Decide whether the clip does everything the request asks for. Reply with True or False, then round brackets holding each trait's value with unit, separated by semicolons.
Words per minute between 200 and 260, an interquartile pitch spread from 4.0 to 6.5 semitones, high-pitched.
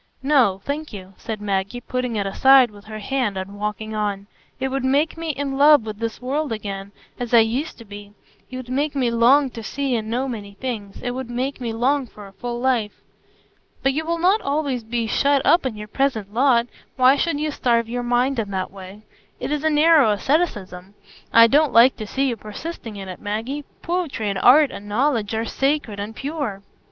True (205 wpm; 4.7 semitones; 240 Hz)